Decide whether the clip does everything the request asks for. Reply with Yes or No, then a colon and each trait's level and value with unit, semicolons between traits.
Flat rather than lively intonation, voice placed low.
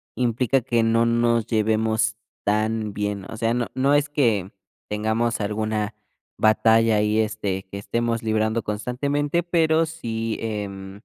Yes: narrow, 1.9 semitones; low, 110 Hz